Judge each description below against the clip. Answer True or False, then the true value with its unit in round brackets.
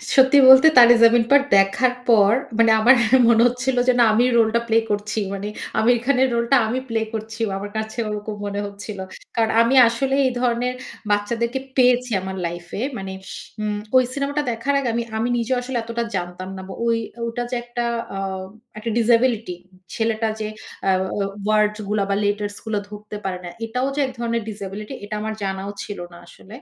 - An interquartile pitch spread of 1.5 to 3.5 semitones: True (2.9 semitones)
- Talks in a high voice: True (225 Hz)